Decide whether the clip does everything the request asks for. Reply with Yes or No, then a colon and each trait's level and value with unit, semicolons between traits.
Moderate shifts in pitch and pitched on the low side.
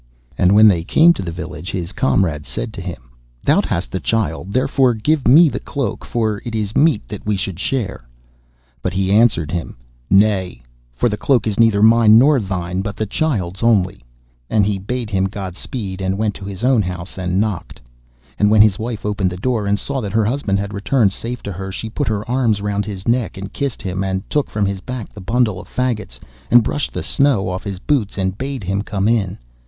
Yes: average, 3.7 semitones; low, 105 Hz